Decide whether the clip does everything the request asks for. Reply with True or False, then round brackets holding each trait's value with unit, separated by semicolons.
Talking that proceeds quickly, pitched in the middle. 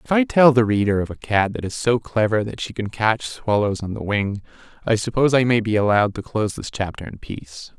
False (245 wpm; 110 Hz)